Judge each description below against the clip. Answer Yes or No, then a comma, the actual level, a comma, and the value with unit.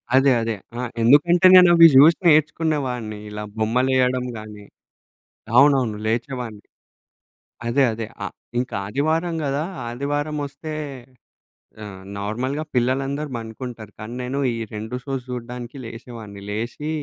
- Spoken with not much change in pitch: No, average, 4.1 semitones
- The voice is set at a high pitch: No, low, 125 Hz